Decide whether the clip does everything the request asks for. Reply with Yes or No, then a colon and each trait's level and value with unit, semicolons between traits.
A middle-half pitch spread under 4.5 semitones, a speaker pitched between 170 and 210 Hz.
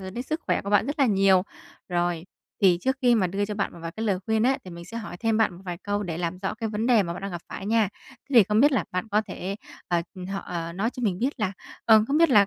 Yes: average, 3.8 semitones; high, 205 Hz